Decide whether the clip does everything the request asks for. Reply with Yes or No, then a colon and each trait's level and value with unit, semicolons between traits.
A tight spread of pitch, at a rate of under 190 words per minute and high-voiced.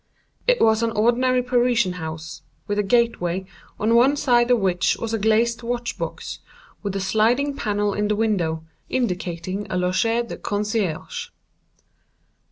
No: average, 4.0 semitones; average, 150 wpm; high, 215 Hz